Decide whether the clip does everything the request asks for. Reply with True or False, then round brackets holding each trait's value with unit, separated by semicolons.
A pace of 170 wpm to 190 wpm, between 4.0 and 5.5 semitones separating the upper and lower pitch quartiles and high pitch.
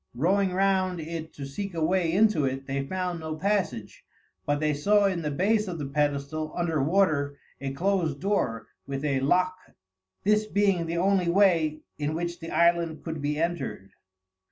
False (175 wpm; 4.3 semitones; 165 Hz)